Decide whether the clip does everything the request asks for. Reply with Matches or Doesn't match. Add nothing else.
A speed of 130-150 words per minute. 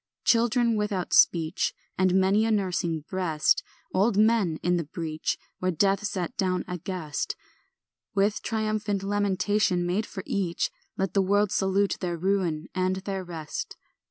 Matches